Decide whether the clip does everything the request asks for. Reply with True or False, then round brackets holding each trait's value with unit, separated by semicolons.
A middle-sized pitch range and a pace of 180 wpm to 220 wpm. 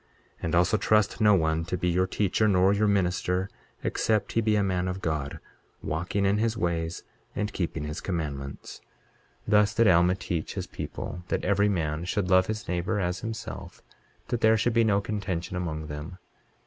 True (3.5 semitones; 185 wpm)